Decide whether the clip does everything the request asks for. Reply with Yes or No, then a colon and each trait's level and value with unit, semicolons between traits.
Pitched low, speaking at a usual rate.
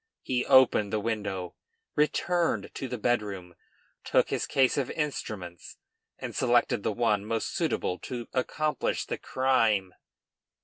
No: low, 115 Hz; slow, 130 wpm